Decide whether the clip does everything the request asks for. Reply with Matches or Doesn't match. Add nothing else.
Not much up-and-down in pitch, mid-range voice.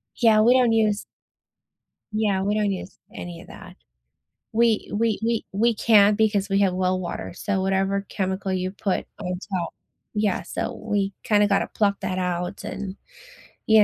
Doesn't match